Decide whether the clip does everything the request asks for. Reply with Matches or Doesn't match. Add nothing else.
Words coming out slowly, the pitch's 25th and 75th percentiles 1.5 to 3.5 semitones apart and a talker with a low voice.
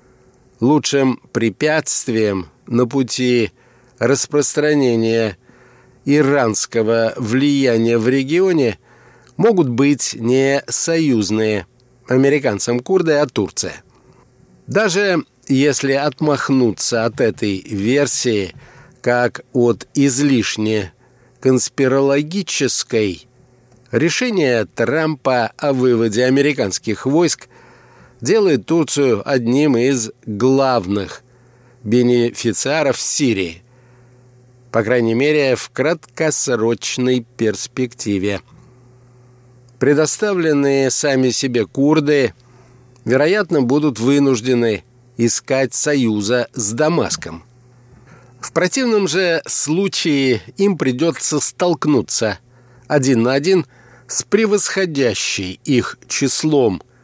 Matches